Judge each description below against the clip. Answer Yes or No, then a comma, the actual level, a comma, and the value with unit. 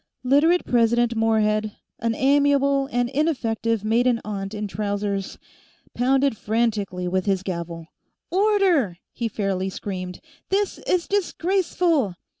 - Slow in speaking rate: Yes, slow, 110 wpm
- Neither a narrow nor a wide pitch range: No, wide, 5.8 semitones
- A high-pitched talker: Yes, high, 230 Hz